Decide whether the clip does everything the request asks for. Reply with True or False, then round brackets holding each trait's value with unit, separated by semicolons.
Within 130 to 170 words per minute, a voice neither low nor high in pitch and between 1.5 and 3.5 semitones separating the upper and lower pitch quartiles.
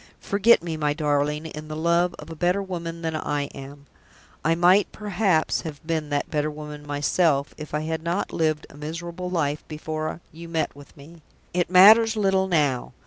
False (185 wpm; 160 Hz; 2.8 semitones)